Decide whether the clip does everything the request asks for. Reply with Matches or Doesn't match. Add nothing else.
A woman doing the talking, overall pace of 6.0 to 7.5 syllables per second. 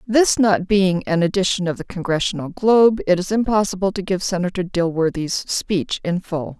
Doesn't match